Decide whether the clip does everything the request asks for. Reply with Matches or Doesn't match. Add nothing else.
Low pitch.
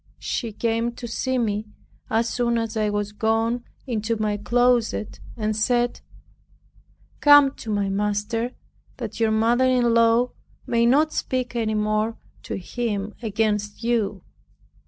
Doesn't match